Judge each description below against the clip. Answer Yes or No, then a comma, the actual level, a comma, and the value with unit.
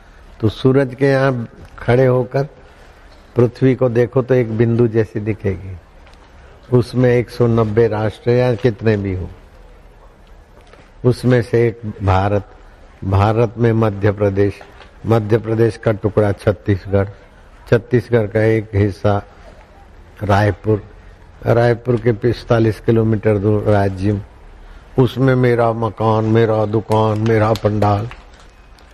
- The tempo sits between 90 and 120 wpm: Yes, slow, 110 wpm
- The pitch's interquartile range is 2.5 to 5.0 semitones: Yes, average, 3.3 semitones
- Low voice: Yes, low, 110 Hz